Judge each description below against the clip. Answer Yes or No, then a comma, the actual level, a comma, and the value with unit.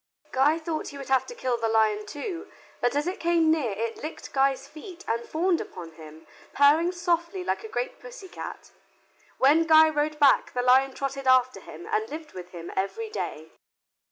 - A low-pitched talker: No, very high, 285 Hz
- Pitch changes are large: Yes, wide, 5.7 semitones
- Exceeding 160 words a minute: Yes, average, 190 wpm